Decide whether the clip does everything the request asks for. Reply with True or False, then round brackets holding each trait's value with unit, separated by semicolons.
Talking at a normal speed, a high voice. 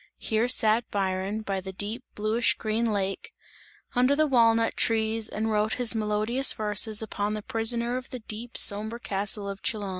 True (170 wpm; 220 Hz)